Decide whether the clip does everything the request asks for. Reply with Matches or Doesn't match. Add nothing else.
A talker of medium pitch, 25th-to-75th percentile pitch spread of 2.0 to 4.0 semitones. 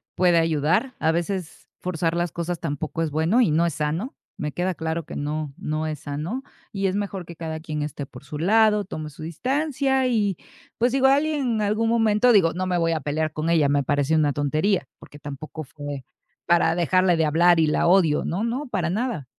Doesn't match